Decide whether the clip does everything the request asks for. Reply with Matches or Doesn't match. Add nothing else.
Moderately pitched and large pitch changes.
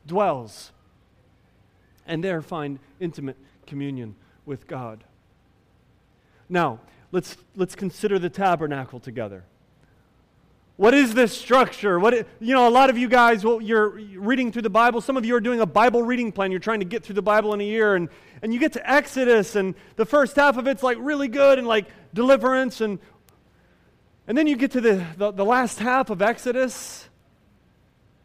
Doesn't match